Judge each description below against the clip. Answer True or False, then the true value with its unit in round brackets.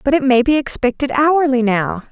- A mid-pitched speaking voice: False (265 Hz)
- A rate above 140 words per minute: True (200 wpm)